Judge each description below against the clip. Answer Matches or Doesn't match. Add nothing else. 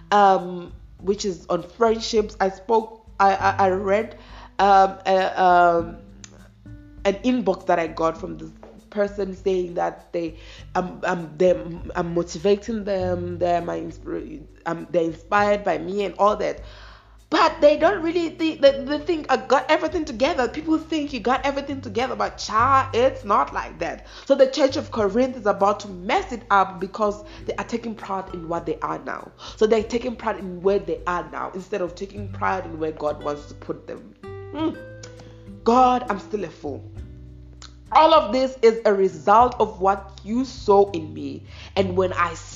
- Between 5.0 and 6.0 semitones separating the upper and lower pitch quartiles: Matches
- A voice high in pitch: Matches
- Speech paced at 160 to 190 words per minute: Matches